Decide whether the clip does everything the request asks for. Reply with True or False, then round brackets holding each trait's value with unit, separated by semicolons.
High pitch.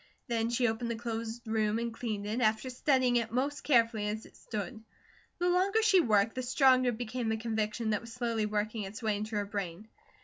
True (230 Hz)